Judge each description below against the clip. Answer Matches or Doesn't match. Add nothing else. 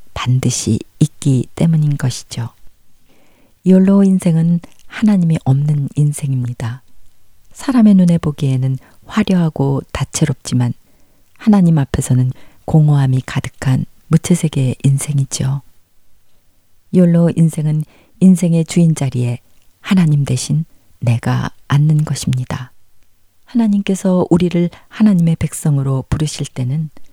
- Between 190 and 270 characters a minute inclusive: Matches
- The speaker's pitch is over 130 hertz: Matches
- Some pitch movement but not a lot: Matches